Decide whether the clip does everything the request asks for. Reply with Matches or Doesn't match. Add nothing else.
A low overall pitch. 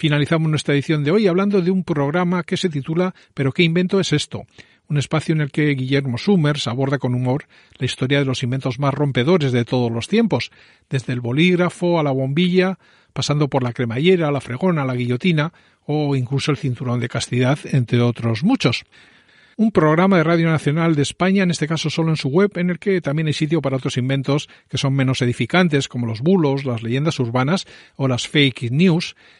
Doesn't match